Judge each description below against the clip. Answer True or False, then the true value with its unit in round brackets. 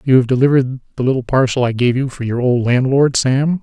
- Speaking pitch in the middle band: False (130 Hz)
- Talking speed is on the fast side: True (230 wpm)